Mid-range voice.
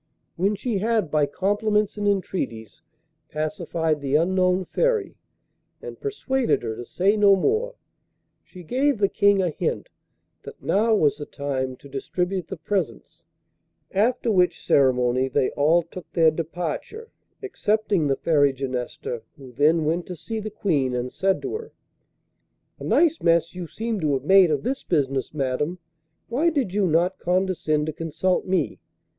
Yes: medium, 180 Hz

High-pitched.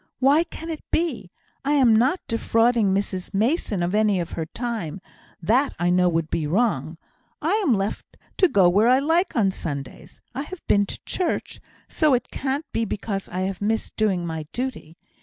Yes: high, 215 Hz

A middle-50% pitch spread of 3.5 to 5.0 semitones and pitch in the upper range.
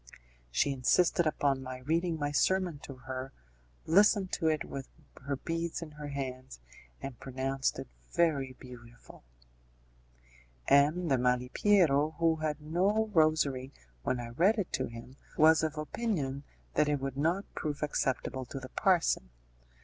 No: average, 3.9 semitones; medium, 145 Hz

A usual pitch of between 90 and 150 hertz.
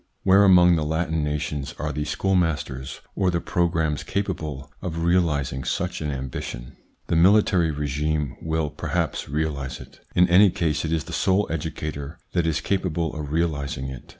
No: very low, 80 Hz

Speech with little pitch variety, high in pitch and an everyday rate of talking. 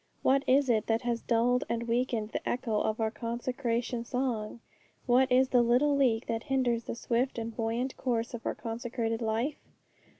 Yes: narrow, 1.9 semitones; high, 235 Hz; average, 175 wpm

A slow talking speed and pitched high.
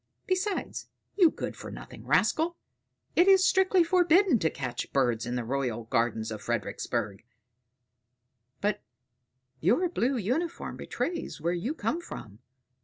Yes: slow, 130 wpm; high, 225 Hz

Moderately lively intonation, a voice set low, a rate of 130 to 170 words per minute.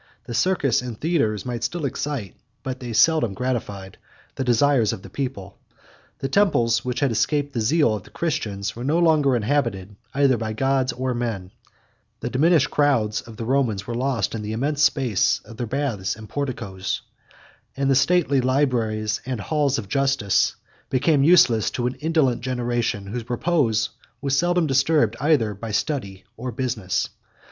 Yes: average, 4.4 semitones; low, 125 Hz; average, 165 wpm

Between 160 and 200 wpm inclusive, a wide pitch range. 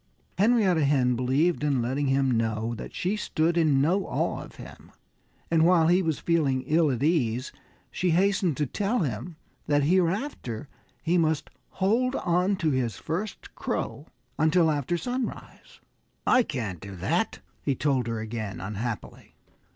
No: average, 150 wpm; wide, 5.9 semitones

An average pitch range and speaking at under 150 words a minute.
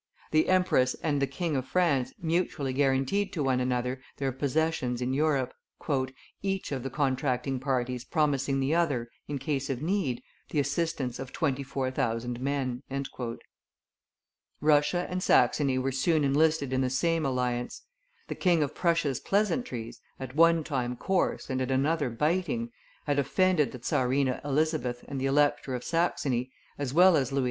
No: average, 3.8 semitones; average, 160 wpm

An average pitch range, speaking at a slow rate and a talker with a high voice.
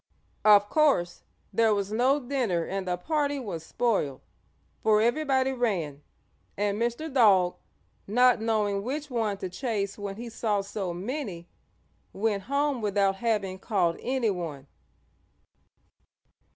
Yes: average, 4.4 semitones; slow, 125 wpm; high, 210 Hz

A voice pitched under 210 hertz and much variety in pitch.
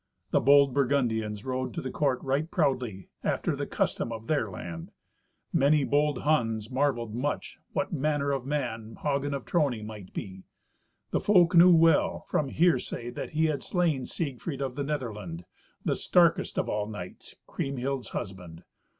No: low, 135 Hz; average, 4.7 semitones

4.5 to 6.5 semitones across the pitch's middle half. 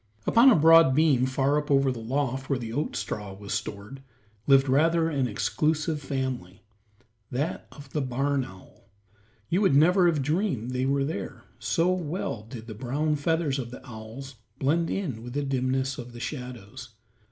No: average, 3.7 semitones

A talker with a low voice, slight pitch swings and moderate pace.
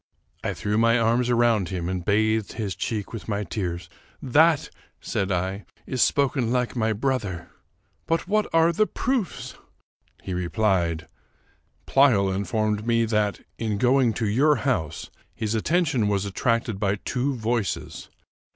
No: low, 110 Hz; average, 4.1 semitones; average, 150 wpm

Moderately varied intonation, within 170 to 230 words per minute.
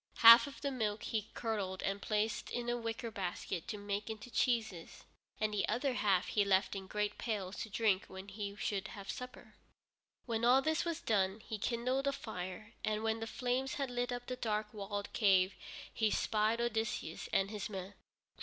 Yes: average, 3.1 semitones; average, 185 wpm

